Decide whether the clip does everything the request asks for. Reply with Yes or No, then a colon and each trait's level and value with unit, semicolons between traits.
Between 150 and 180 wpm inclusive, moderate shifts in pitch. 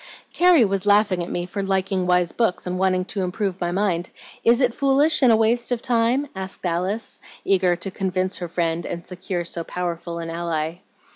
No: average, 195 wpm; average, 3.9 semitones